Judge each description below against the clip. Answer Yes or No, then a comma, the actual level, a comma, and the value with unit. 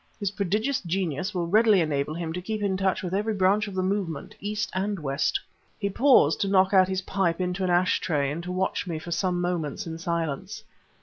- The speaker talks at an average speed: No, fast, 210 wpm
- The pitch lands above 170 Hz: Yes, medium, 185 Hz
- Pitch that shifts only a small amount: No, average, 3.0 semitones